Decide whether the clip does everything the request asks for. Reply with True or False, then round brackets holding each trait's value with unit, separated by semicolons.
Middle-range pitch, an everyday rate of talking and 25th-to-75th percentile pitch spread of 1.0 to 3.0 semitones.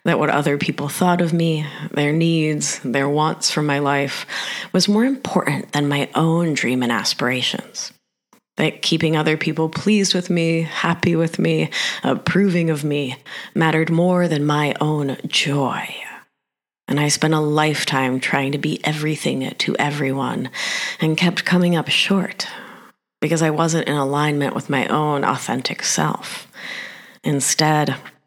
True (155 Hz; 145 wpm; 2.7 semitones)